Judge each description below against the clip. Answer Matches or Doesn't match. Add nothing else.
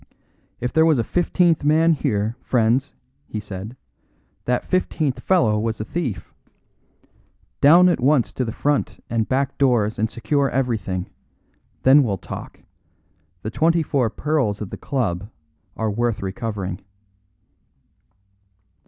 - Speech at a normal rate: Doesn't match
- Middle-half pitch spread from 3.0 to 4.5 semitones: Doesn't match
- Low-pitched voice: Matches